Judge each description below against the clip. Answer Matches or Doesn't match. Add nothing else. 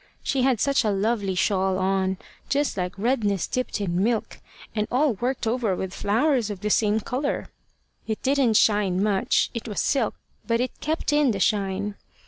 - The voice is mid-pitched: Doesn't match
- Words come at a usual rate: Matches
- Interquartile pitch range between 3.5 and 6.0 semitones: Matches